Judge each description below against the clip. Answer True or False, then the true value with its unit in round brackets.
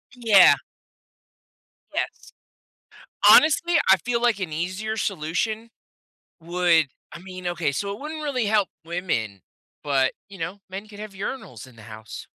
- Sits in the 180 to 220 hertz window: True (190 Hz)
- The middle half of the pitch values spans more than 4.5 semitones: True (5.1 semitones)